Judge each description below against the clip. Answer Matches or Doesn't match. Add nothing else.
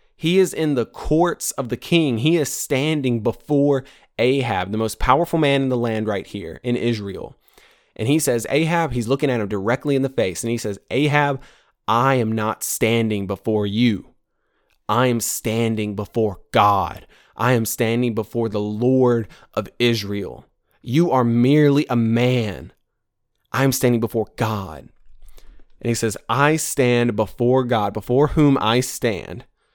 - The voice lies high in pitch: Doesn't match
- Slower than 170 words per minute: Matches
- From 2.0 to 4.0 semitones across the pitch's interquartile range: Matches